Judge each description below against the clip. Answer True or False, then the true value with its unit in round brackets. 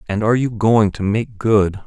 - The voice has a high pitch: False (105 Hz)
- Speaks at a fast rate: True (225 wpm)